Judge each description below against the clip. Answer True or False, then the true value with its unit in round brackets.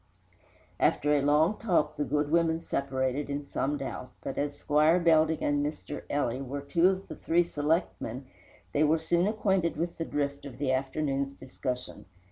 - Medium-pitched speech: True (145 Hz)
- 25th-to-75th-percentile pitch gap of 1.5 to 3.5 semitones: True (2.9 semitones)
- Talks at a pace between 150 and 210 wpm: True (170 wpm)